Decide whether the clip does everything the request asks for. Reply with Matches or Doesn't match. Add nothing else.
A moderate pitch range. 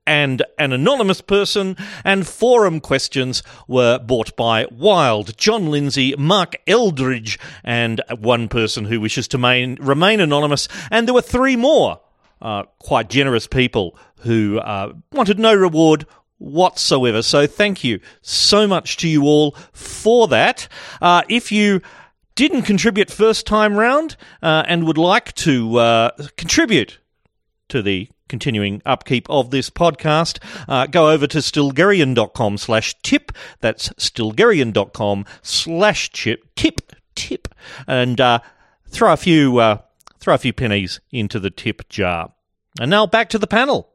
Doesn't match